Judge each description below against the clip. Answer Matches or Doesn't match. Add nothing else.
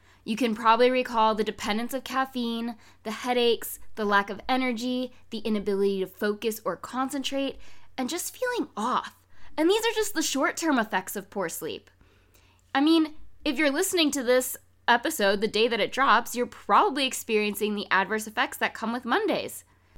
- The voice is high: Matches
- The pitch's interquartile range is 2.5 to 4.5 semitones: Matches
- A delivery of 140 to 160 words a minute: Doesn't match